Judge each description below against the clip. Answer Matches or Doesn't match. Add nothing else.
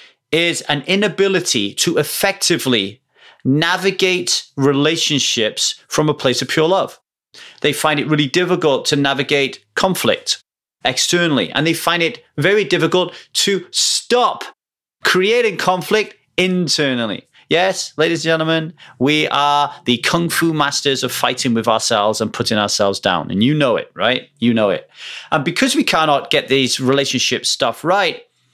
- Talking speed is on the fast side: Doesn't match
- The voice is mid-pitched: Matches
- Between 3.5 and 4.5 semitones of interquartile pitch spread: Doesn't match